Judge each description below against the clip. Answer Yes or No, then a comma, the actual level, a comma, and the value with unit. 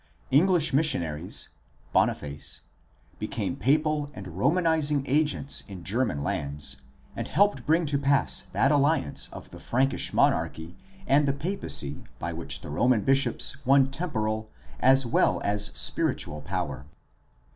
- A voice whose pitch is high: No, low, 135 Hz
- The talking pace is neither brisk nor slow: No, slow, 125 wpm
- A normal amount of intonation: No, wide, 8.7 semitones